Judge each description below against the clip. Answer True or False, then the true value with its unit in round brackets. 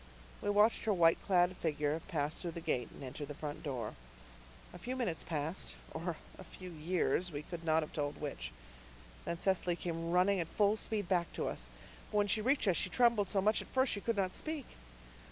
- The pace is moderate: False (215 wpm)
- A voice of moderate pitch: True (175 Hz)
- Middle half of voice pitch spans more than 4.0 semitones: True (4.4 semitones)